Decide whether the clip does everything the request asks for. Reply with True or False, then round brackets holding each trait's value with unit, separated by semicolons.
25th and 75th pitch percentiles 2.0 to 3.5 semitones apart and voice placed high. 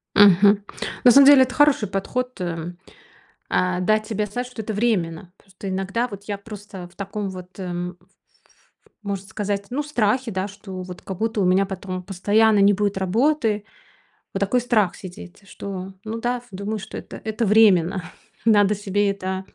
True (2.7 semitones; 200 Hz)